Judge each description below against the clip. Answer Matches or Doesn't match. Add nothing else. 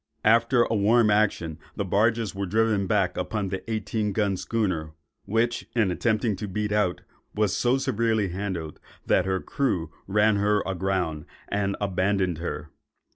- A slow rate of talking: Doesn't match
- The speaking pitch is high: Doesn't match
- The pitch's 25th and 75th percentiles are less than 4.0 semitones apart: Matches